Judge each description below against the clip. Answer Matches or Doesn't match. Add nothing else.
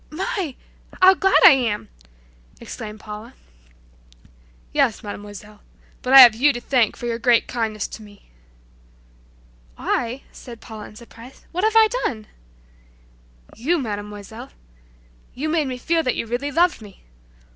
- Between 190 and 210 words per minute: Doesn't match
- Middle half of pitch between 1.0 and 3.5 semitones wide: Doesn't match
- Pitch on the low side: Doesn't match